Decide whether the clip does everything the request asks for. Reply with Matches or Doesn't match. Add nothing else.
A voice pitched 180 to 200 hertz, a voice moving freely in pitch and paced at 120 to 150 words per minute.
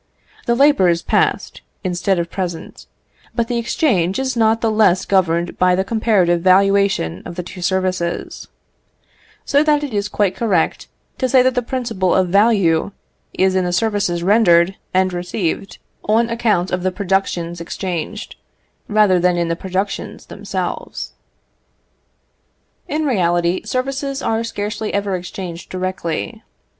Doesn't match